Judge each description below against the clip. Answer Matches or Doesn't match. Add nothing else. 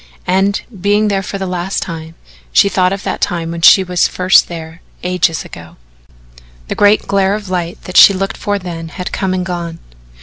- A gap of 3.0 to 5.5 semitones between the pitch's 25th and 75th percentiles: Doesn't match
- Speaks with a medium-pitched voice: Matches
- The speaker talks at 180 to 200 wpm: Matches